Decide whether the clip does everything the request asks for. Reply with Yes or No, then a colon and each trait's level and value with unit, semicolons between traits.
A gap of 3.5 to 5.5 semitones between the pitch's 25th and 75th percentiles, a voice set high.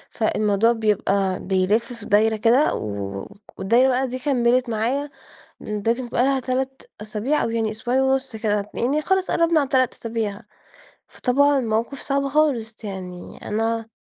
Yes: average, 3.8 semitones; high, 230 Hz